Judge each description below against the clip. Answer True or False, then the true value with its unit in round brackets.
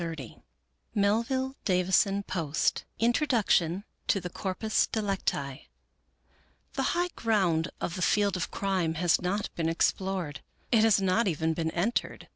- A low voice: False (190 Hz)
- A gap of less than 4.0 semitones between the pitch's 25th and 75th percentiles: False (4.4 semitones)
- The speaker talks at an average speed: False (130 wpm)